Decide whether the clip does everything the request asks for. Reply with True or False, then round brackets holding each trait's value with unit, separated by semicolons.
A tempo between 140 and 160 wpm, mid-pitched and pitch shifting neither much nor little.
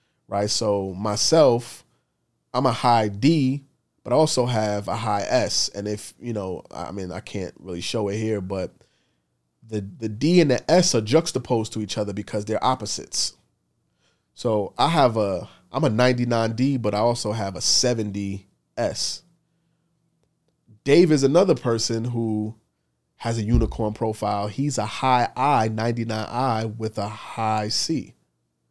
False (150 wpm; 110 Hz; 3.6 semitones)